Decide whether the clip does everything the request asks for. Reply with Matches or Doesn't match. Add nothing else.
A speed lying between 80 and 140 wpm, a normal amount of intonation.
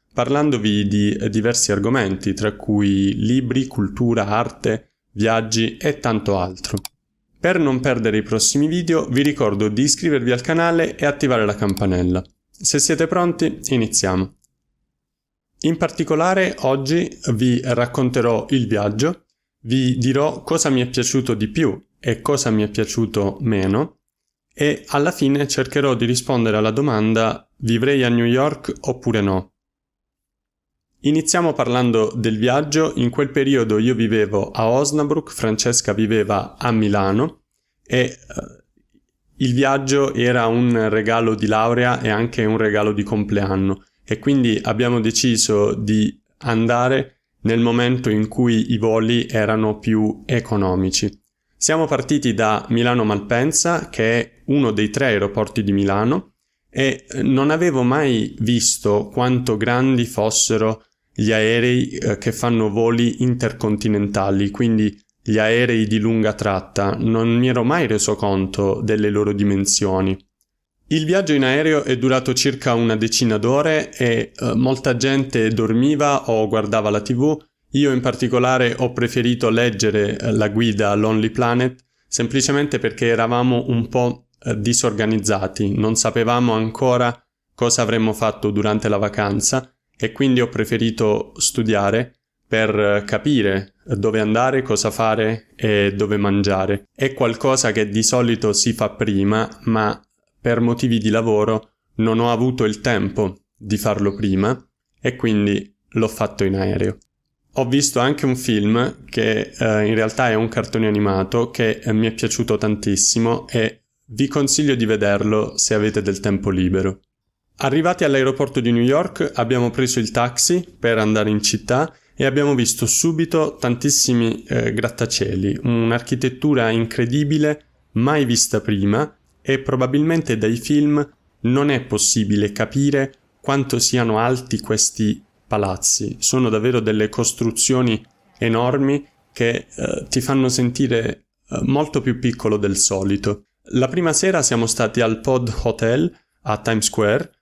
Matches